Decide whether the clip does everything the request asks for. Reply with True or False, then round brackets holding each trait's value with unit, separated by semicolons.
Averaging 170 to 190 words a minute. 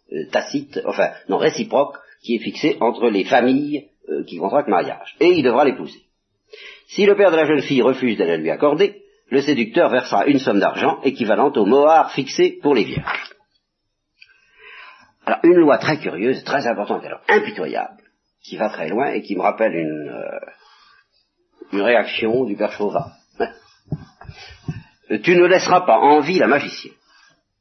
False (160 wpm)